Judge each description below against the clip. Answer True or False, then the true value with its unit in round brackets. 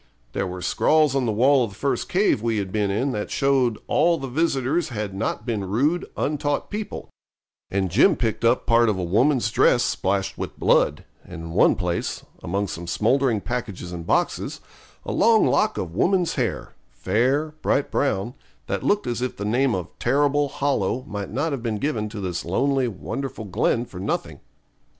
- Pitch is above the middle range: False (120 Hz)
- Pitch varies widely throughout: True (5.8 semitones)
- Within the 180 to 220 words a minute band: True (185 wpm)